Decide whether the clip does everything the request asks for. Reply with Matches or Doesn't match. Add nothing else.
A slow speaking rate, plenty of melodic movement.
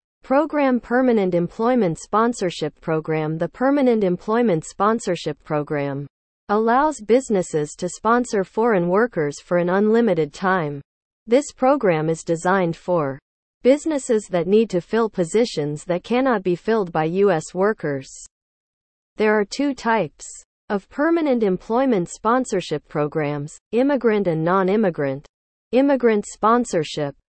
Matches